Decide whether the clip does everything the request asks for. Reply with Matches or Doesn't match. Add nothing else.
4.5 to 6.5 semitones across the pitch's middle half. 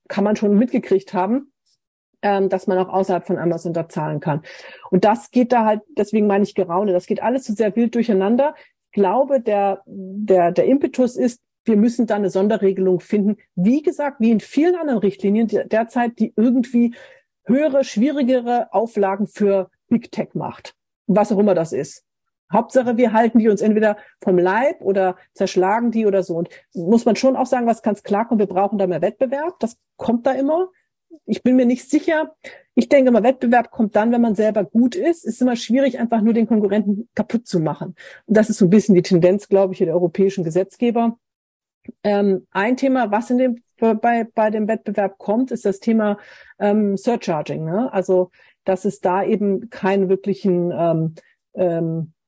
Doesn't match